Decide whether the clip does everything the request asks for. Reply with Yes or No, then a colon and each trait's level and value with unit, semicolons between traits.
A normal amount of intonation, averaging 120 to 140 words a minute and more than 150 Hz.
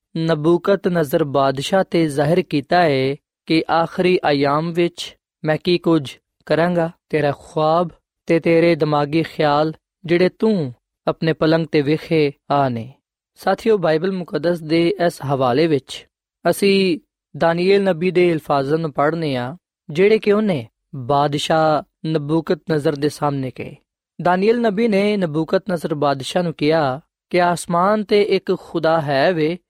Yes: average, 3.1 semitones; average, 130 wpm; medium, 165 Hz